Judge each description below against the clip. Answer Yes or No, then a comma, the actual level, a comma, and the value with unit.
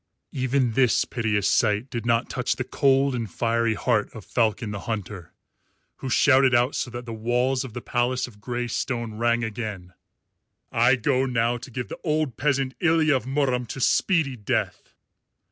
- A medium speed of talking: Yes, average, 175 wpm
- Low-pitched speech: Yes, low, 120 Hz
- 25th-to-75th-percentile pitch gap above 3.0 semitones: No, narrow, 2.6 semitones